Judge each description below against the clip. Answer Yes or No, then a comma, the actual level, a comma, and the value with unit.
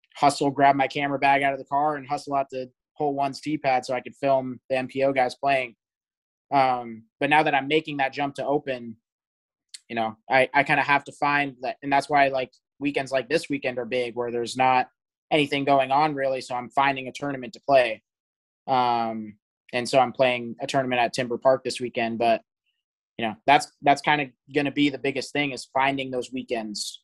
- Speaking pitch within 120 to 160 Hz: Yes, low, 135 Hz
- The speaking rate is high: Yes, fast, 215 wpm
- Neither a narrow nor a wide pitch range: No, narrow, 2.3 semitones